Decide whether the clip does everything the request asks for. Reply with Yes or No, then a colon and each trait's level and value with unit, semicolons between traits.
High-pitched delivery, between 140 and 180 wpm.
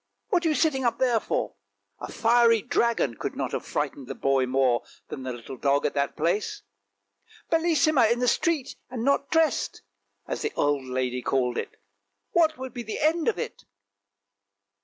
No: high, 230 Hz; average, 195 wpm